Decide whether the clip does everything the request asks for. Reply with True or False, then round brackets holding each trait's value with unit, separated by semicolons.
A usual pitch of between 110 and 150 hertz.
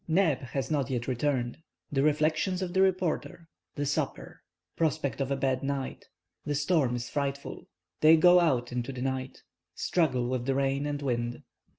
True (140 Hz)